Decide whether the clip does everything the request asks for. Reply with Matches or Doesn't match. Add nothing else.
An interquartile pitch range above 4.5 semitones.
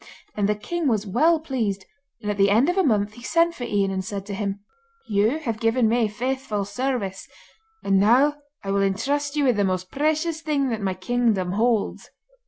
Matches